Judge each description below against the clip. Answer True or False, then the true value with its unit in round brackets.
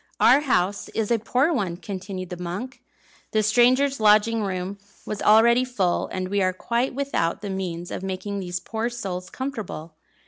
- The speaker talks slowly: False (170 wpm)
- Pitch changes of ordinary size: True (4.4 semitones)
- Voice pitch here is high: True (205 Hz)